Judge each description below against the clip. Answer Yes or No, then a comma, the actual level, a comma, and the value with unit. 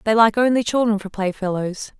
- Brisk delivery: No, average, 180 wpm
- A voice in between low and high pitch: No, high, 210 Hz